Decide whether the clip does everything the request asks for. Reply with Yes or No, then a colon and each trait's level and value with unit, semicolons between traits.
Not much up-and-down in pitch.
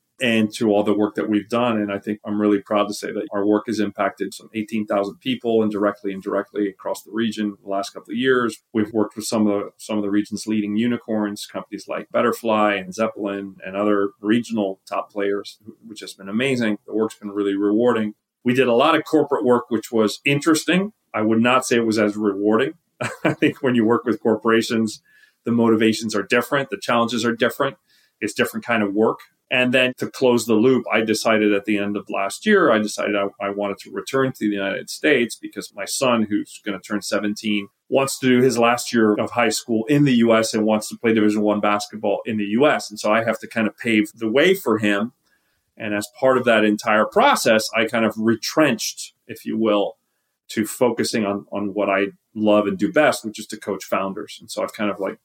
Yes: narrow, 2.3 semitones